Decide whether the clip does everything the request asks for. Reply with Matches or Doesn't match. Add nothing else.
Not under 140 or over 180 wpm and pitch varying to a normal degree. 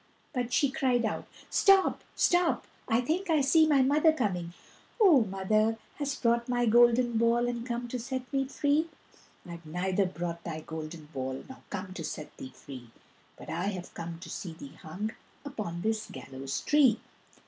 Doesn't match